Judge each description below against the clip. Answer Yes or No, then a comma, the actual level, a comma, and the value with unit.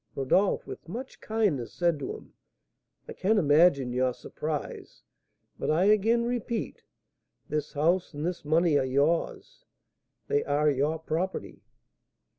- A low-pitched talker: No, medium, 160 Hz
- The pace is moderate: No, slow, 130 wpm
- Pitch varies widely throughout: No, average, 4.7 semitones